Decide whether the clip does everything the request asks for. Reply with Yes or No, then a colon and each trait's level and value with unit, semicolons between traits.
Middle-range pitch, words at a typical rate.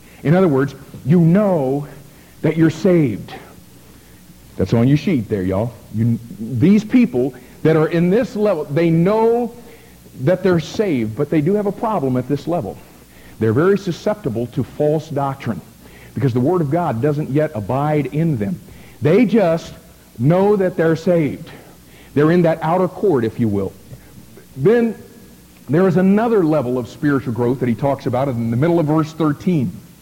Yes: medium, 150 Hz; average, 170 wpm